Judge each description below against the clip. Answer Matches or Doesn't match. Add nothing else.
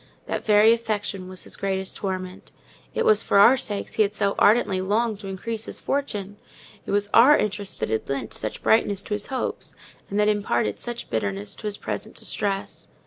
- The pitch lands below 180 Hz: Doesn't match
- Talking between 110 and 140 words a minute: Doesn't match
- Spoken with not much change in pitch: Matches